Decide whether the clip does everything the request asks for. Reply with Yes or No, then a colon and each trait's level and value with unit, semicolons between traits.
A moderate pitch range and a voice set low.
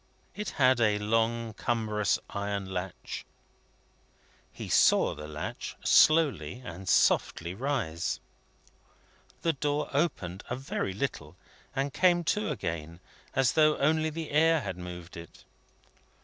No: wide, 8.5 semitones; low, 115 Hz